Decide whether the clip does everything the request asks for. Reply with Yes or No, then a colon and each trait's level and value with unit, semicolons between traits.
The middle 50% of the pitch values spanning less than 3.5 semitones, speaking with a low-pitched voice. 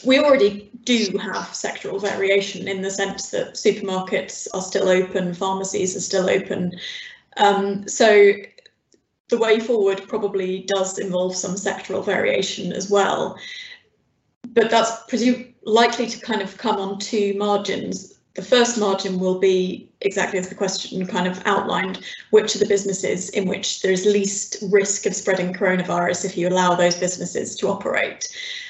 No: narrow, 2.4 semitones; high, 200 Hz